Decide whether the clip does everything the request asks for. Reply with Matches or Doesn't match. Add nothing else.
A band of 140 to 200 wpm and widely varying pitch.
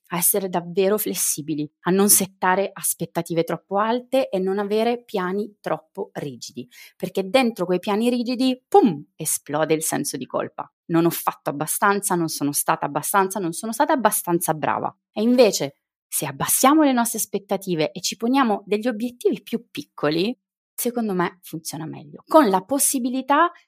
Matches